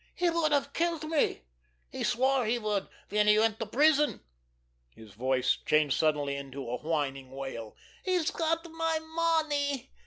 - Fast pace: No, average, 155 wpm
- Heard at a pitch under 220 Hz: No, high, 235 Hz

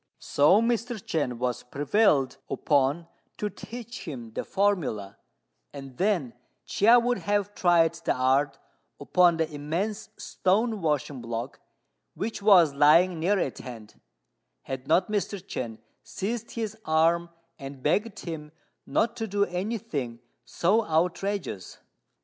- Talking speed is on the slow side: Yes, slow, 130 wpm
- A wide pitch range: Yes, wide, 6.7 semitones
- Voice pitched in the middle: Yes, medium, 170 Hz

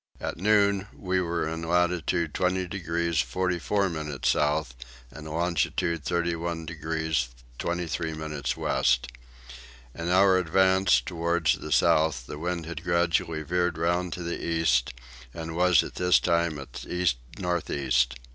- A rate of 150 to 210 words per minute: No, slow, 135 wpm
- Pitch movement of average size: No, narrow, 2.3 semitones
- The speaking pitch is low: Yes, very low, 85 Hz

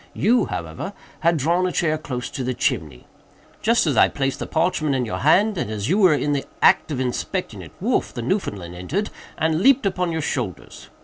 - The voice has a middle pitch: Yes, medium, 150 Hz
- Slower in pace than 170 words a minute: No, fast, 205 wpm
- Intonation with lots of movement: Yes, wide, 6.6 semitones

